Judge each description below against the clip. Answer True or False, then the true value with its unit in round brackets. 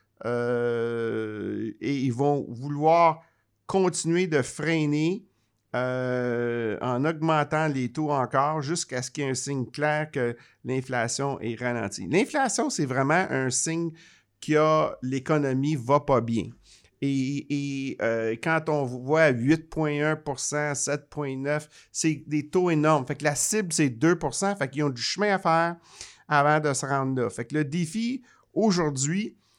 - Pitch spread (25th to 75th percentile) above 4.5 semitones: False (3.9 semitones)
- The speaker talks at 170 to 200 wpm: False (145 wpm)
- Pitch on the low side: False (145 Hz)